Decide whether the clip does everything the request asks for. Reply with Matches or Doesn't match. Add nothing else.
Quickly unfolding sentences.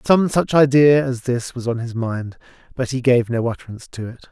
Matches